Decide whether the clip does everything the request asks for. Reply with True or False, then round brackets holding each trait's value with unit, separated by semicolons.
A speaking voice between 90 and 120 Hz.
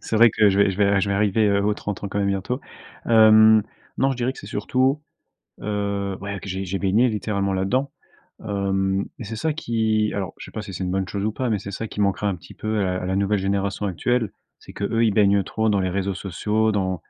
True (100 Hz)